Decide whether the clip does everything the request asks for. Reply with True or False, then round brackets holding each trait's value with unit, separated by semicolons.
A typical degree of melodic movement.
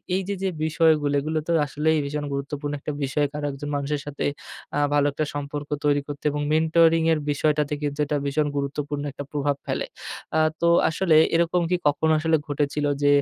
False (1.7 semitones)